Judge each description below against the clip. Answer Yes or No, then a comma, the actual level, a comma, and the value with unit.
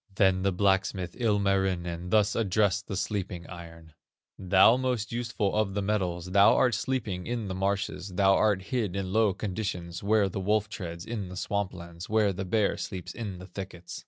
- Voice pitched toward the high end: No, very low, 95 Hz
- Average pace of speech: Yes, average, 180 wpm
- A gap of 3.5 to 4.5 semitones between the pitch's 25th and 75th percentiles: No, average, 2.7 semitones